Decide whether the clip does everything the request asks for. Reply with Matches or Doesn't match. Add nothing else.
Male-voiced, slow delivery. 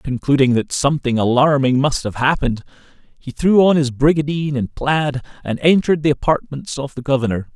Doesn't match